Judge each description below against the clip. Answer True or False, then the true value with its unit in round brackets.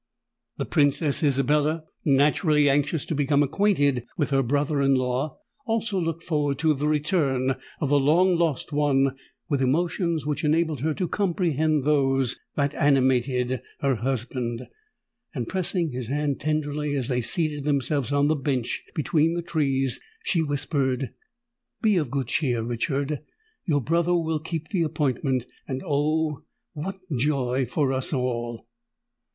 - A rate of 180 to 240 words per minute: False (145 wpm)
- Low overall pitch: False (145 Hz)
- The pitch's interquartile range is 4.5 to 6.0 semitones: False (2.9 semitones)